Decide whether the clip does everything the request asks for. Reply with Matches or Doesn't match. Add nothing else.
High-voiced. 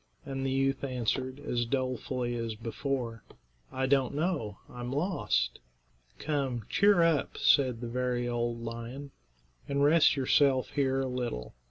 Doesn't match